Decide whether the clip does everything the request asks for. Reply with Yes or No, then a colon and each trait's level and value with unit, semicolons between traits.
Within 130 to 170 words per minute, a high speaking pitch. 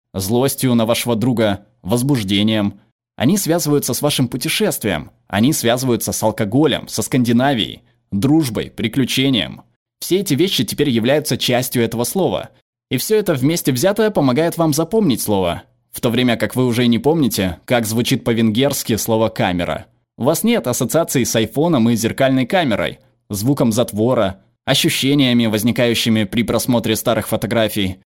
No: average, 140 wpm; low, 120 Hz